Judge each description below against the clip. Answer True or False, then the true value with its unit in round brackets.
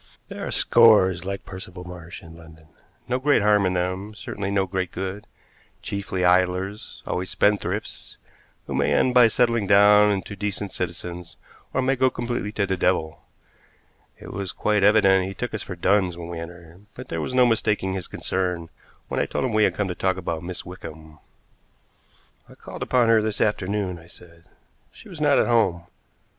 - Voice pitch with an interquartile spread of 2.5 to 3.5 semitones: True (3.1 semitones)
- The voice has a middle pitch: False (95 Hz)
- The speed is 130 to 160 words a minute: False (185 wpm)